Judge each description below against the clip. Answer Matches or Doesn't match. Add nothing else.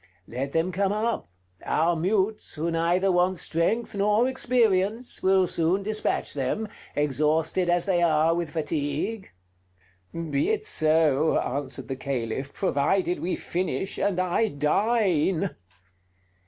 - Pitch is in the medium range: Matches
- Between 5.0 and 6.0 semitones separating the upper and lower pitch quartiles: Doesn't match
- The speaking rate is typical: Doesn't match